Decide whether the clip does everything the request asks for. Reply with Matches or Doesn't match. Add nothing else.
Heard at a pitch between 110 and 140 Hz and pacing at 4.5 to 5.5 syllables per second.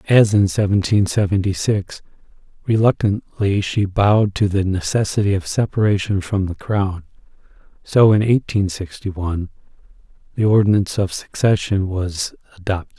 Doesn't match